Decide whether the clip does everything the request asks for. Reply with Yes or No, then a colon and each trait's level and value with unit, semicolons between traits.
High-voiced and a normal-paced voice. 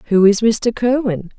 Yes: high, 215 Hz; average, 175 wpm